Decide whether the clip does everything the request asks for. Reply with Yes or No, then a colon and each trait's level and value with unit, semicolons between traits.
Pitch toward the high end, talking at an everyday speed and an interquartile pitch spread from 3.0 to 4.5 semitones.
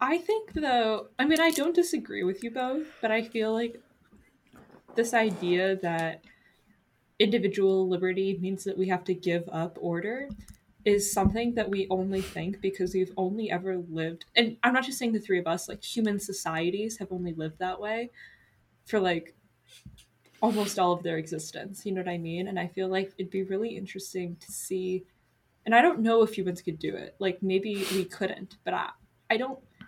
Yes: high, 195 Hz; average, 190 wpm; average, 3.6 semitones